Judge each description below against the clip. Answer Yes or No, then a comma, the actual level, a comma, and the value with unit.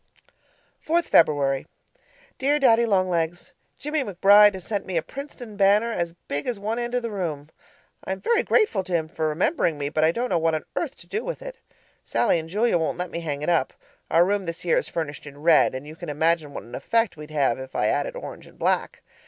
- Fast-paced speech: Yes, fast, 230 wpm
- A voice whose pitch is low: No, medium, 175 Hz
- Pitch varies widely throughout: Yes, wide, 6.6 semitones